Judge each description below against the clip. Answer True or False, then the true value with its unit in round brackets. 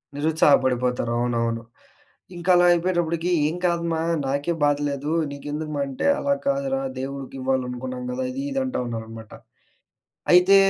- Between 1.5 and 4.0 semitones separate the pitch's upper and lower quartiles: False (5.5 semitones)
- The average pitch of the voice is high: False (150 Hz)